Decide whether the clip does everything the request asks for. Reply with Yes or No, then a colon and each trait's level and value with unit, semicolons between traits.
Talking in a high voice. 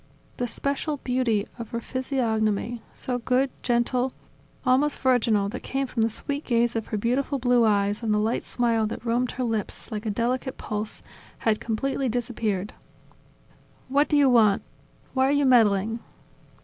Yes: high, 240 Hz